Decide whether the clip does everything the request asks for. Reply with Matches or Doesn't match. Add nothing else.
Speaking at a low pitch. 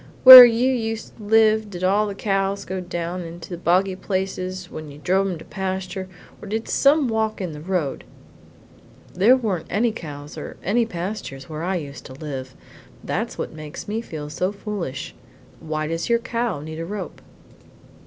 Doesn't match